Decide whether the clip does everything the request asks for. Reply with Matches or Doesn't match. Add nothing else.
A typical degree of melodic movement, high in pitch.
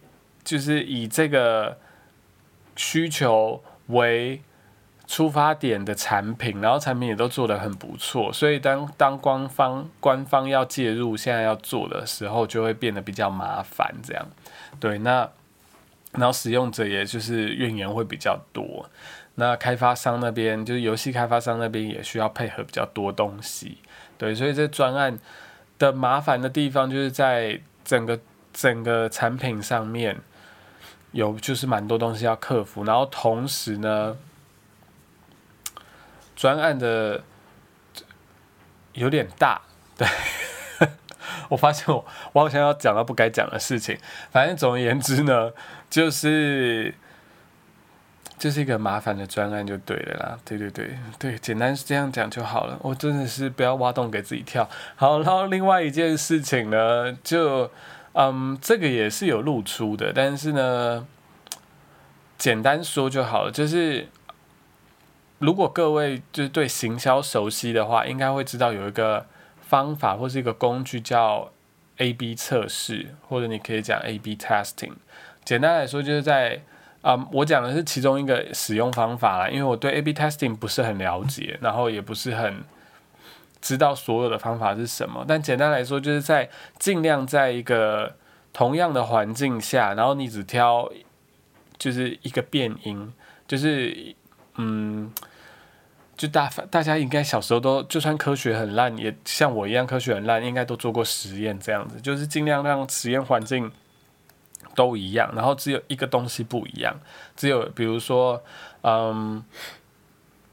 Doesn't match